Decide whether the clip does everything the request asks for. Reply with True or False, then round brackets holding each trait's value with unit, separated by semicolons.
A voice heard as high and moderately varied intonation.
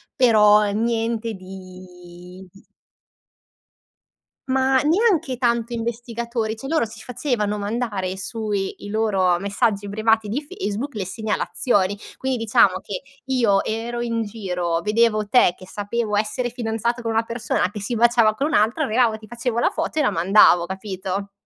True (220 Hz; 3.0 semitones)